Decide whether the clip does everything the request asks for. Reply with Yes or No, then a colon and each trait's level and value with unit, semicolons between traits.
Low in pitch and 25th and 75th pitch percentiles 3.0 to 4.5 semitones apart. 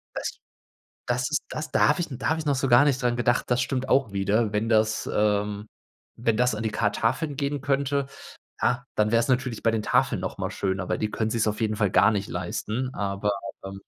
Yes: low, 115 Hz; average, 3.7 semitones